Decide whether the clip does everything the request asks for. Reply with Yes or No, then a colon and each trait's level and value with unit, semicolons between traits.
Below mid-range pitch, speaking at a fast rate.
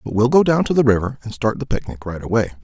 Yes: low, 120 Hz; fast, 295 wpm